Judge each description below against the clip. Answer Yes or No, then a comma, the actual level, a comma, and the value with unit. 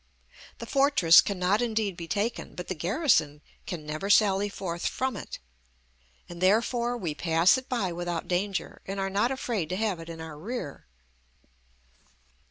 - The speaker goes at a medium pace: Yes, average, 160 wpm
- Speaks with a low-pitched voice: No, high, 195 Hz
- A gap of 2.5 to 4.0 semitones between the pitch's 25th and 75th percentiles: No, average, 4.7 semitones